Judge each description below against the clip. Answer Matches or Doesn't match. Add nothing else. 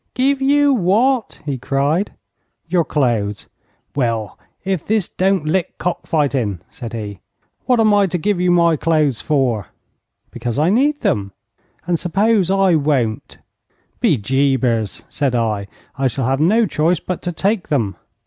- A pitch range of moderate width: Doesn't match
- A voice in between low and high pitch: Matches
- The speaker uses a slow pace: Doesn't match